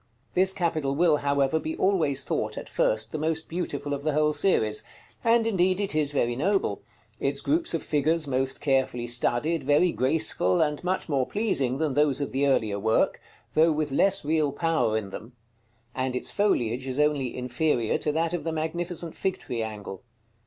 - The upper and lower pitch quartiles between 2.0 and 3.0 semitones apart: No, average, 4.1 semitones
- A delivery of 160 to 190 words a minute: Yes, average, 180 wpm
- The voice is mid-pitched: Yes, medium, 150 Hz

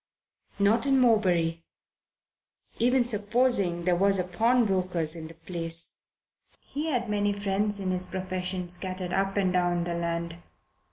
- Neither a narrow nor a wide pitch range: Yes, average, 3.2 semitones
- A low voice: No, medium, 185 Hz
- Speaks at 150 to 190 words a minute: No, slow, 135 wpm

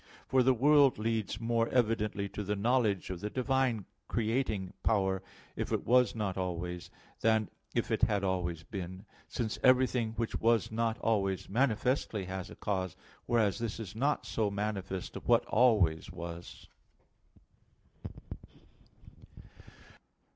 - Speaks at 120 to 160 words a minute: Yes, slow, 135 wpm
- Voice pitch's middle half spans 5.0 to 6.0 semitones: No, average, 3.6 semitones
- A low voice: Yes, low, 110 Hz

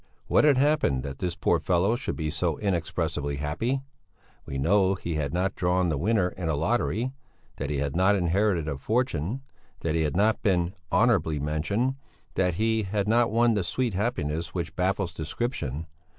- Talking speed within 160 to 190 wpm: Yes, average, 180 wpm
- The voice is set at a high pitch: No, very low, 90 Hz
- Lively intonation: Yes, wide, 5.7 semitones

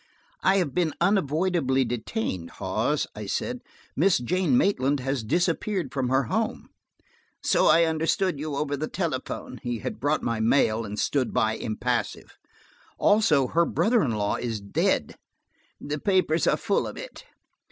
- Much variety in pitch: Yes, wide, 6.6 semitones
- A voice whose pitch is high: No, medium, 145 Hz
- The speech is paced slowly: No, average, 150 wpm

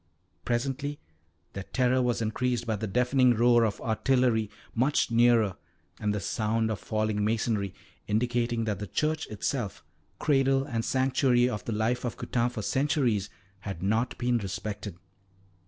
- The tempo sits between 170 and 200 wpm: No, average, 145 wpm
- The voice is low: Yes, low, 115 Hz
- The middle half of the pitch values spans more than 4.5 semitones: No, average, 2.8 semitones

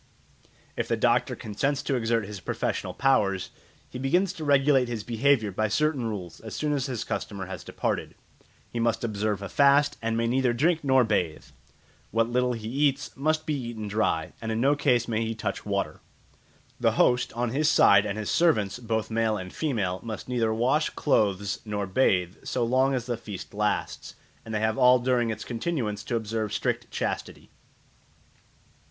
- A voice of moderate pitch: No, low, 115 Hz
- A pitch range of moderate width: Yes, average, 3.8 semitones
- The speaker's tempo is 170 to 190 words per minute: Yes, average, 180 wpm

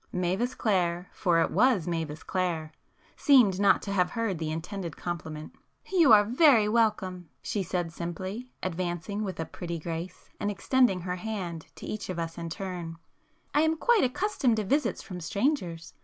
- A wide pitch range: No, average, 4.5 semitones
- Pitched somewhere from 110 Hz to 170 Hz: No, medium, 185 Hz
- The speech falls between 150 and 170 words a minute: Yes, average, 160 wpm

